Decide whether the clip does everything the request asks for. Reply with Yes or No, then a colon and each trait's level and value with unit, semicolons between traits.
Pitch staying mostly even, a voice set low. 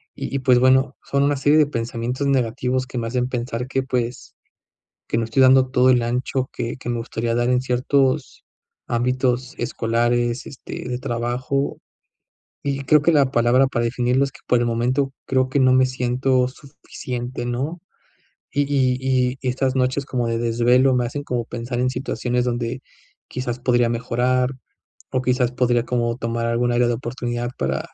Yes: narrow, 1.5 semitones; low, 125 Hz